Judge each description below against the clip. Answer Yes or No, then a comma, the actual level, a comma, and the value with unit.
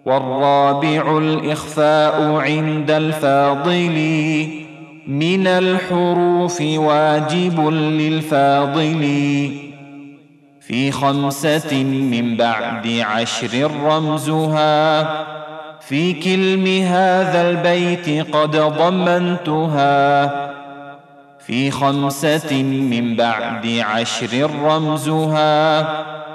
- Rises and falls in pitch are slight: Yes, narrow, 1.9 semitones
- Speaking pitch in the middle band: Yes, medium, 155 Hz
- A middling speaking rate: No, slow, 60 wpm